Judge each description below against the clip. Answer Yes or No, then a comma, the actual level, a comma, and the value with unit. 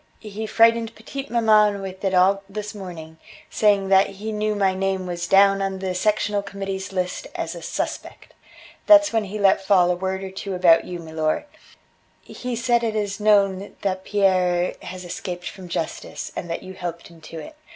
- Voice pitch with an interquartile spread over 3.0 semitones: No, narrow, 2.6 semitones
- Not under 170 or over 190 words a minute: Yes, average, 185 wpm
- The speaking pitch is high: Yes, high, 195 Hz